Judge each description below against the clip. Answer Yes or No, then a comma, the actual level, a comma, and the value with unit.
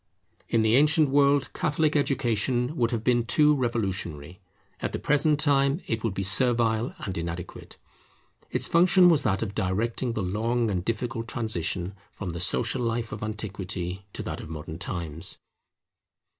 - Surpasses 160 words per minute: No, average, 155 wpm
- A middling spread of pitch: No, wide, 5.8 semitones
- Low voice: Yes, low, 115 Hz